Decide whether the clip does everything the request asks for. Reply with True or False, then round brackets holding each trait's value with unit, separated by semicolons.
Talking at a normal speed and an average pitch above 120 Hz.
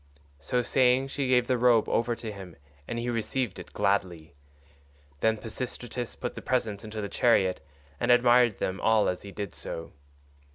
False (170 wpm; 115 Hz)